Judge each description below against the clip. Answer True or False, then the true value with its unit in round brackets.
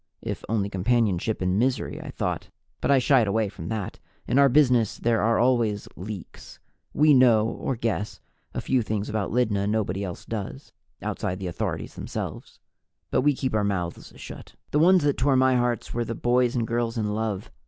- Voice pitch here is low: True (115 Hz)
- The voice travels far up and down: False (3.5 semitones)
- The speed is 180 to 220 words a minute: True (185 wpm)